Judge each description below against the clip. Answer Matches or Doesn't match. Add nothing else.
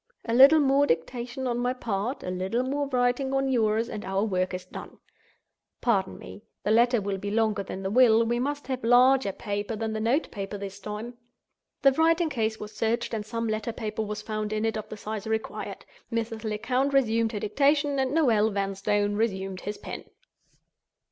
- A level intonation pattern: Doesn't match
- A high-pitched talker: Matches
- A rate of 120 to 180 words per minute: Doesn't match